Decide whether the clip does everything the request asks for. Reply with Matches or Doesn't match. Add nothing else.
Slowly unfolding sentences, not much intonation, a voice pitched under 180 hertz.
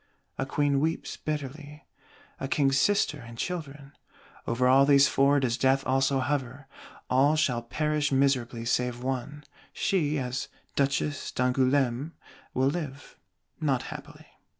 Matches